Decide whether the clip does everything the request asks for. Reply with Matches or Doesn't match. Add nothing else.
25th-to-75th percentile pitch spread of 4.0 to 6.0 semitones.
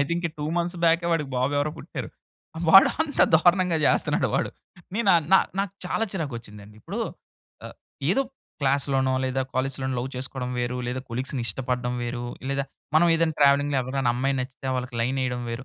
Matches